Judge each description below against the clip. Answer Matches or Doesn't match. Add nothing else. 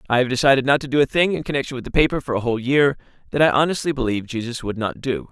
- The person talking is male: Matches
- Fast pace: Matches